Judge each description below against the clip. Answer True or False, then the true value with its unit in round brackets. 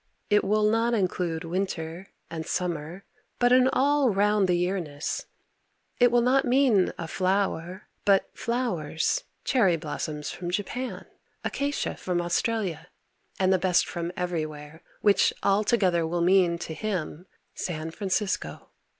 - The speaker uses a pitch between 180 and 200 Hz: True (185 Hz)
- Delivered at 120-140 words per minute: True (135 wpm)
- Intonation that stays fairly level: False (4.1 semitones)